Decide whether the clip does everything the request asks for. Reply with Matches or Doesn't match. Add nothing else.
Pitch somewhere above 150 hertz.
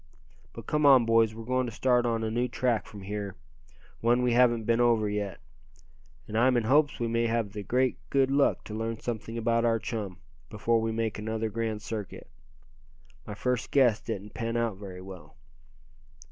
Doesn't match